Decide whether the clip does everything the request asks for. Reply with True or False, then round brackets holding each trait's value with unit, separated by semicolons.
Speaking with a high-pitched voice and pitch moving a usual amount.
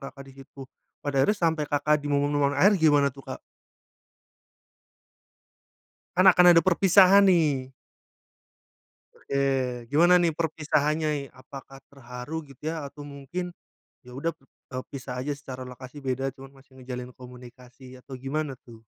False (140 Hz; 3.3 semitones)